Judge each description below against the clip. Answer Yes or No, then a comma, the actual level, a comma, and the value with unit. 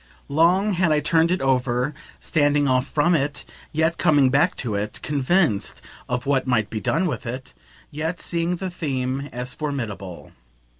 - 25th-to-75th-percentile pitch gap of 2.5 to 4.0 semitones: No, average, 4.6 semitones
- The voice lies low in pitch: No, medium, 145 Hz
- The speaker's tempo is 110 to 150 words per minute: No, average, 160 wpm